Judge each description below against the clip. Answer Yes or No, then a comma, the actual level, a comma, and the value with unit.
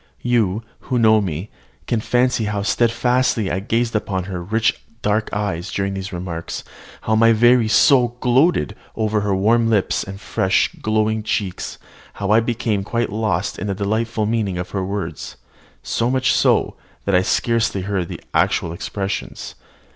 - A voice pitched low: Yes, low, 105 Hz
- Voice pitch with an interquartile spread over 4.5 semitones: No, average, 3.0 semitones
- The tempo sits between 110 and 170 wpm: Yes, average, 160 wpm